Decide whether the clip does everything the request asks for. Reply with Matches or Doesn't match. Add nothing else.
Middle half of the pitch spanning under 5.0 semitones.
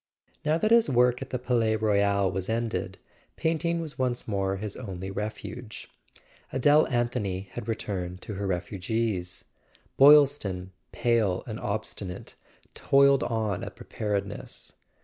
Matches